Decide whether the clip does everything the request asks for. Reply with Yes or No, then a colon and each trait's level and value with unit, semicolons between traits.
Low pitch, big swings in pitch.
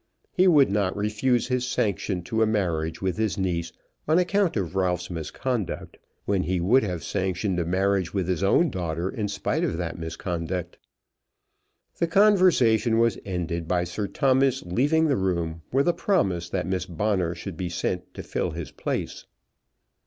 Yes: very low, 95 Hz; wide, 5.8 semitones